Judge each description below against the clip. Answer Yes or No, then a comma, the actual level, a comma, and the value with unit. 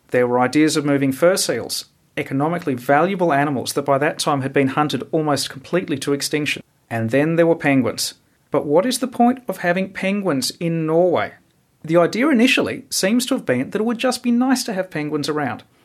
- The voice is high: No, medium, 160 Hz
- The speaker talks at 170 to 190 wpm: No, average, 200 wpm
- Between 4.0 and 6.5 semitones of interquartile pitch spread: Yes, average, 5.2 semitones